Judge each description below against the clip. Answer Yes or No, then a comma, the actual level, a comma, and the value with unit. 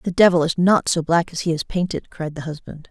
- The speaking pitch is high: No, medium, 165 Hz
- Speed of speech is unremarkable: No, fast, 270 wpm